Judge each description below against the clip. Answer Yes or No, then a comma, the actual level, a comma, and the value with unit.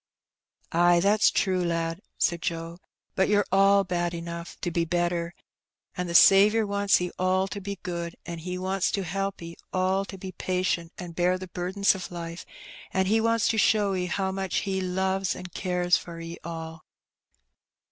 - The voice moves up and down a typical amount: No, narrow, 2.2 semitones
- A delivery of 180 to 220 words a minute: Yes, average, 185 wpm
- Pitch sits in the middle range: Yes, medium, 180 Hz